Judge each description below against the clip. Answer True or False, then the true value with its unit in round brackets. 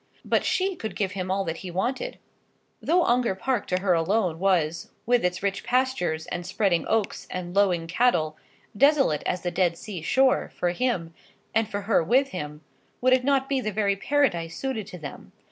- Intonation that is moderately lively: False (6.3 semitones)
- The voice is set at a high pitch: True (195 Hz)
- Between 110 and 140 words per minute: False (190 wpm)